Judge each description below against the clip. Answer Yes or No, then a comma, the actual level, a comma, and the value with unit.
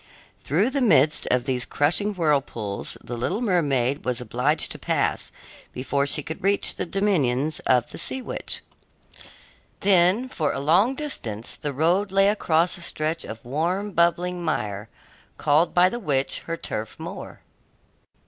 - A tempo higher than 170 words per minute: No, average, 150 wpm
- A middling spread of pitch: No, wide, 6.3 semitones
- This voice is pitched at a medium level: Yes, medium, 160 Hz